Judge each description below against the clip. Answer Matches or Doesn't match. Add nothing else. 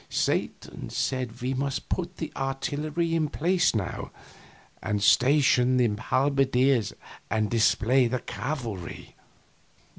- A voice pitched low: Matches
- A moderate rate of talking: Doesn't match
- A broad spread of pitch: Doesn't match